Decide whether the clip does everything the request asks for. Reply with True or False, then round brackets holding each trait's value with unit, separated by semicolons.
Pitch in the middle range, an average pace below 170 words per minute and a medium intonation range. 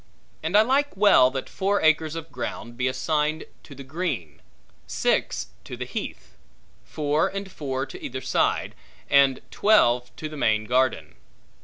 True (150 Hz; 155 wpm; 4.6 semitones)